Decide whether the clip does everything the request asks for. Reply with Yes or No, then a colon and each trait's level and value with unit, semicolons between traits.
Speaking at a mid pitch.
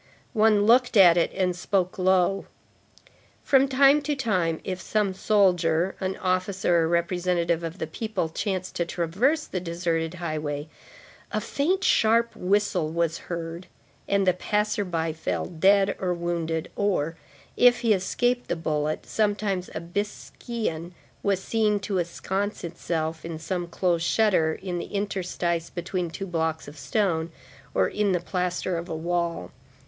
Yes: medium, 180 Hz